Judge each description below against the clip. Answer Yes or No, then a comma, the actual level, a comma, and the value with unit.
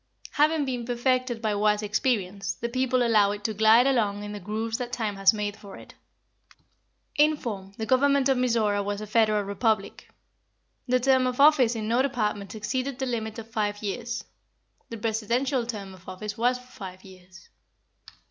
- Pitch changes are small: No, average, 3.5 semitones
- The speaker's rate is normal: Yes, average, 175 wpm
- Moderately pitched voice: No, high, 225 Hz